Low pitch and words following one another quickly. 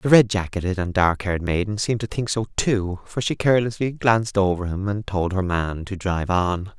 Yes: low, 100 Hz; fast, 220 wpm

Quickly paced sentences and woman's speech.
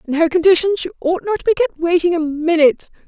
Yes: fast, 235 wpm; female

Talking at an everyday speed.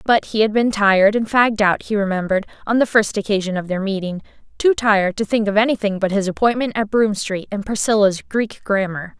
No: fast, 210 wpm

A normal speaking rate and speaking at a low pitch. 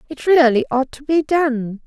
No: average, 195 wpm; very high, 275 Hz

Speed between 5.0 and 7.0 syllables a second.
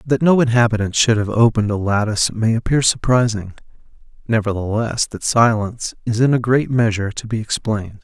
Yes: 5.8 syllables/s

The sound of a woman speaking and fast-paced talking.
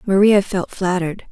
No: female; slow, 135 wpm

